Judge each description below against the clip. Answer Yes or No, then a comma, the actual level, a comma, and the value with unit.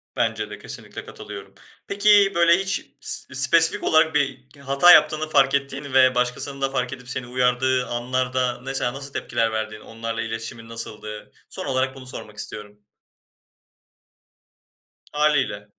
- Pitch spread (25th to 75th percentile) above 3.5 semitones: No, average, 3.0 semitones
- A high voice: No, low, 130 Hz